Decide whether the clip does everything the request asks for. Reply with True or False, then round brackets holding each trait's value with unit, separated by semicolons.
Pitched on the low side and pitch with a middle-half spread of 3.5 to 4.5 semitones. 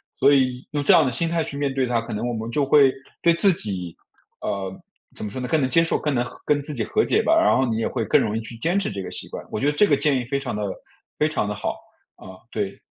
False (130 Hz; 5.0 semitones)